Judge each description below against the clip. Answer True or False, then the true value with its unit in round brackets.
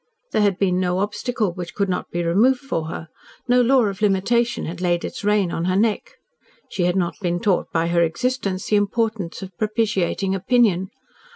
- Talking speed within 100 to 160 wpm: False (190 wpm)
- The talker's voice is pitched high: True (195 Hz)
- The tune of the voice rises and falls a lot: False (3.6 semitones)